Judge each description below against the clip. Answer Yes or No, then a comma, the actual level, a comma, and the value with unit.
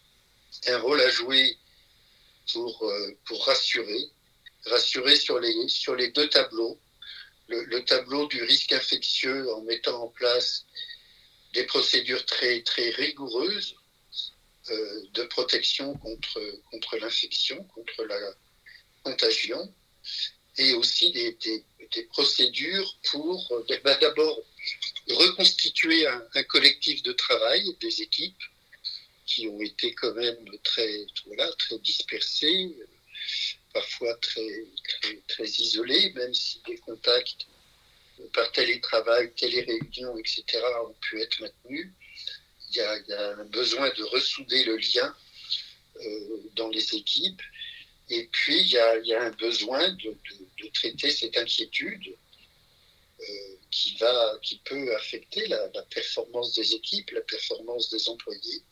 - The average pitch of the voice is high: Yes, very high, 380 Hz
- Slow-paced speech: Yes, slow, 130 wpm